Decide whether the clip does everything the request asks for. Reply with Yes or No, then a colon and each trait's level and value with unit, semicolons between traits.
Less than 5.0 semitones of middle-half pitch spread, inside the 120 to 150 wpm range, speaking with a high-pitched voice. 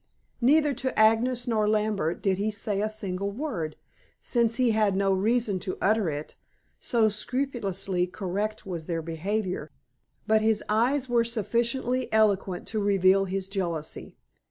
Yes: average, 3.4 semitones; average, 145 wpm; high, 210 Hz